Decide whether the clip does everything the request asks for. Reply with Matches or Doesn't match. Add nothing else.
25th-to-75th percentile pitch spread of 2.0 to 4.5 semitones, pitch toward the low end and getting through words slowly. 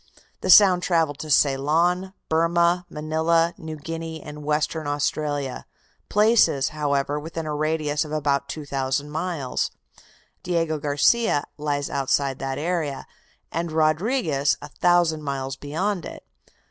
Doesn't match